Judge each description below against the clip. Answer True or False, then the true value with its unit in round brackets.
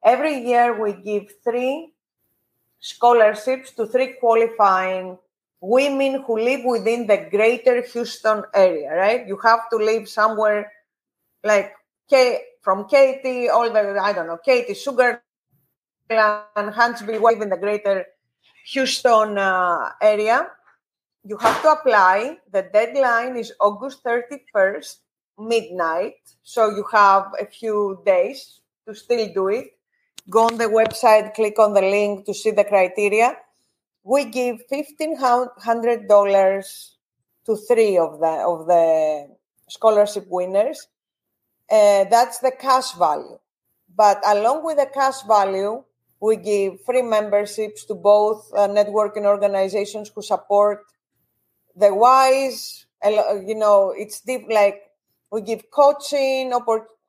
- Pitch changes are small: False (3.4 semitones)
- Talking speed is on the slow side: True (125 wpm)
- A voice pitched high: True (220 Hz)